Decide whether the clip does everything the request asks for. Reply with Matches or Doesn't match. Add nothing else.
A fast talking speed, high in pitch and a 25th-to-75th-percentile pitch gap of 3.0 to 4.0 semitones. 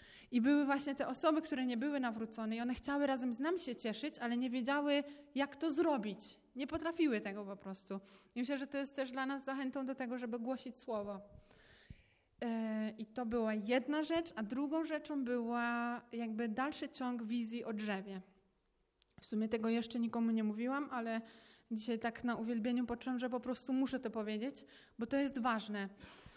Matches